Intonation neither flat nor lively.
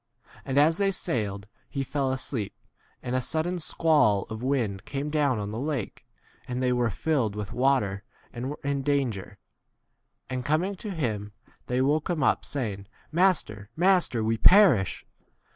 No: wide, 5.9 semitones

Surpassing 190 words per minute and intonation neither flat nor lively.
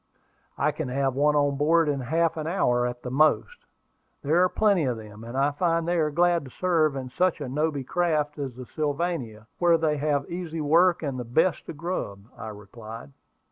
Yes: fast, 205 wpm; average, 4.6 semitones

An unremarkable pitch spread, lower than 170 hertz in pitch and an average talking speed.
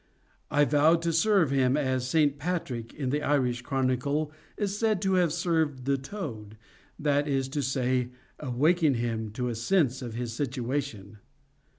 Yes: average, 3.9 semitones; medium, 140 Hz; average, 155 wpm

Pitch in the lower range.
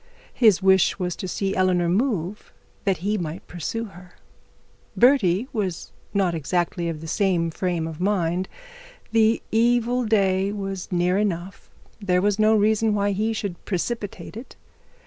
No: high, 195 Hz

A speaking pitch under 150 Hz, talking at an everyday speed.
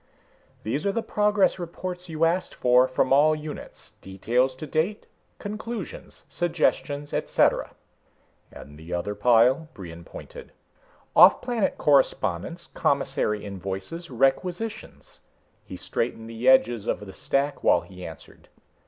No: medium, 140 Hz; slow, 125 wpm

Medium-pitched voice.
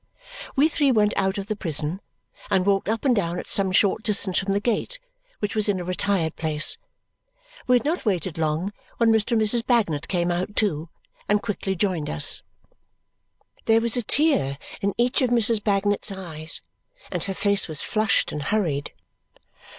No: high, 200 Hz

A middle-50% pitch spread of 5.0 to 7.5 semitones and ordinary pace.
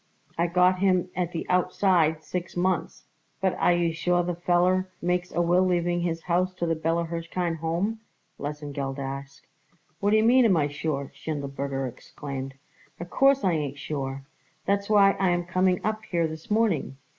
No: average, 3.1 semitones; average, 170 wpm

